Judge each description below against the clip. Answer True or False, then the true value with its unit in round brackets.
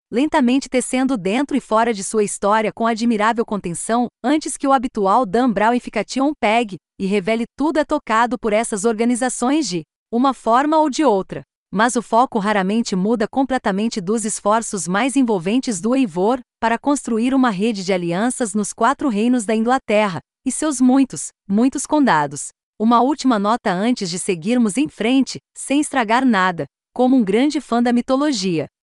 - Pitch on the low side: False (235 Hz)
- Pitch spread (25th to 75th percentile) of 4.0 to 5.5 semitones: False (3.5 semitones)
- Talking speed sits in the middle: True (165 wpm)